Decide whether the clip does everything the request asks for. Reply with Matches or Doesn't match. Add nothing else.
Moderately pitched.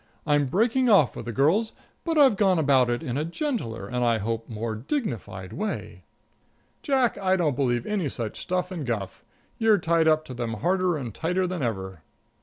Matches